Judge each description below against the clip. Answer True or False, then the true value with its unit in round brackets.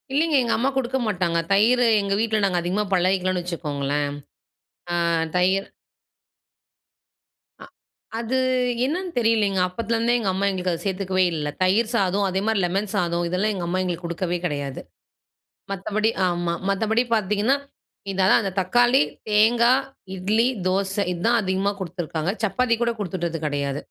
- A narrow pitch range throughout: False (3.9 semitones)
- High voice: True (195 Hz)